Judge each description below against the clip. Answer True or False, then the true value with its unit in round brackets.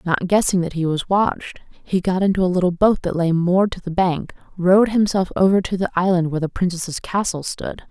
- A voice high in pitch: False (180 Hz)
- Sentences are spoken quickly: True (220 wpm)